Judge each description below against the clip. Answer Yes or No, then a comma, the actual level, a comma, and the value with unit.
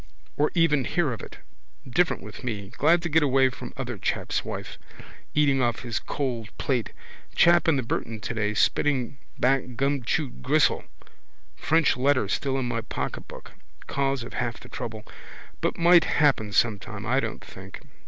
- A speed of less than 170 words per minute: Yes, average, 160 wpm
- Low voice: Yes, low, 130 Hz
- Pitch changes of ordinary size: Yes, average, 4.0 semitones